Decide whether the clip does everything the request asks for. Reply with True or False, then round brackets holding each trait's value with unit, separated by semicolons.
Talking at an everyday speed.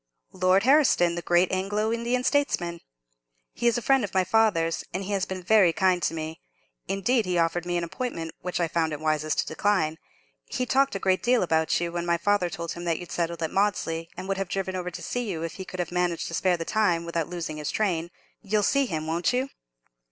False (230 wpm)